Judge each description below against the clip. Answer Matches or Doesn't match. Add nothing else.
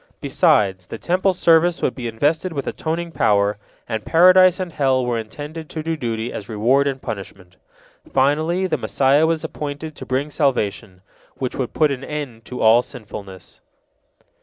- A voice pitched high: Doesn't match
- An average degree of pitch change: Doesn't match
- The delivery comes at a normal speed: Matches